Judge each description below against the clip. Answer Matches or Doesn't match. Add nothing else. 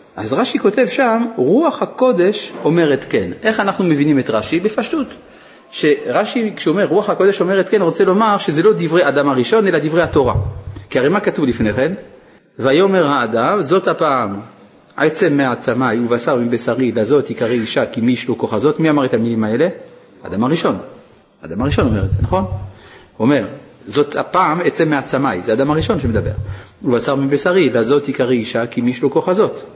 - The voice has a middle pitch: Matches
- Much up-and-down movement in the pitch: Matches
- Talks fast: Matches